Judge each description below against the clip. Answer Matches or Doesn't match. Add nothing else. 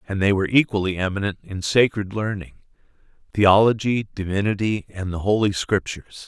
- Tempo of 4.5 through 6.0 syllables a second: Matches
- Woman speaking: Doesn't match